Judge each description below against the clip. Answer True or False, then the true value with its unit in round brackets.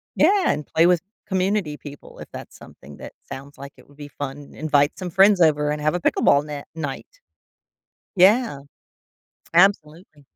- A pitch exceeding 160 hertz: False (150 Hz)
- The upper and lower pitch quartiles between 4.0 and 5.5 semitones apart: True (4.3 semitones)